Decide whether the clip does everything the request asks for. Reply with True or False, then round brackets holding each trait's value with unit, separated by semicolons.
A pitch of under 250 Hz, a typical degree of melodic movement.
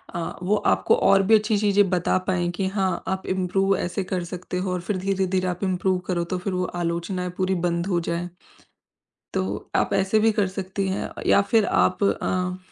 False (185 Hz; 1.5 semitones)